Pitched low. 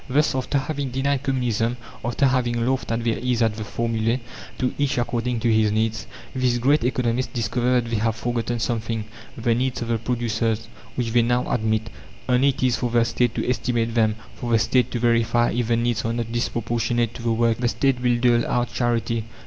Yes: low, 120 Hz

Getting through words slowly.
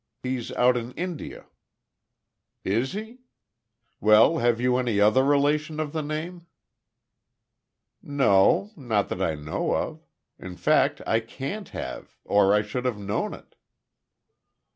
Yes: slow, 130 wpm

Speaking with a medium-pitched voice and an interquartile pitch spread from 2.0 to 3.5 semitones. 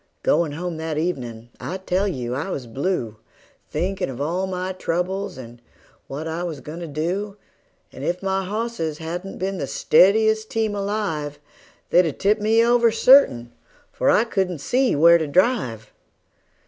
No: medium, 180 Hz; average, 5.0 semitones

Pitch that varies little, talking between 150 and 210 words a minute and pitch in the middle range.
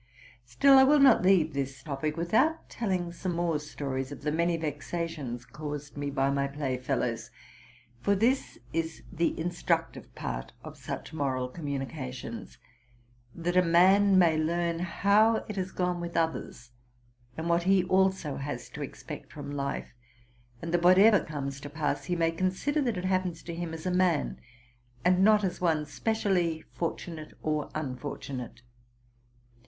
No: average, 4.3 semitones; average, 155 wpm; medium, 165 Hz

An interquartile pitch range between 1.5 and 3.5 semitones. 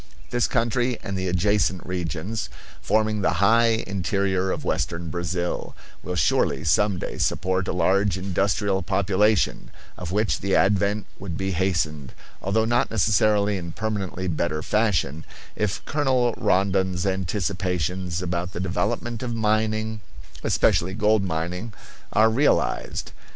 Yes: average, 3.0 semitones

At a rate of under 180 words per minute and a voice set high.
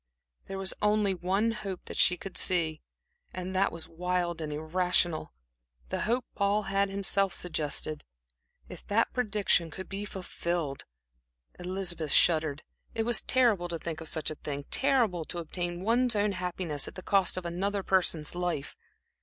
No: average, 160 wpm; medium, 180 Hz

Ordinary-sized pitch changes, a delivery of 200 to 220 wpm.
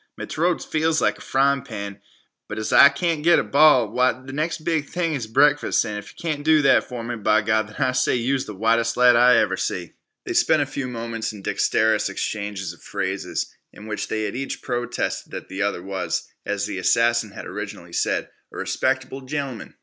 Yes: average, 4.6 semitones; fast, 205 wpm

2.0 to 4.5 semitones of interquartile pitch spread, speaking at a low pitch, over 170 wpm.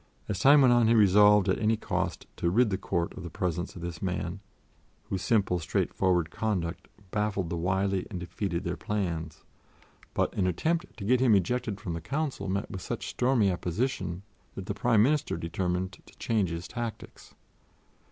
Yes: average, 4.1 semitones; very low, 95 Hz; average, 180 wpm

